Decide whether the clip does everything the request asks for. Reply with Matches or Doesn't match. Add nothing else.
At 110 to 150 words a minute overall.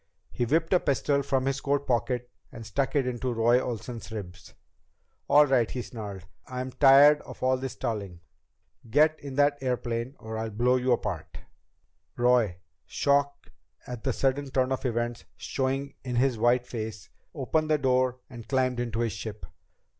Doesn't match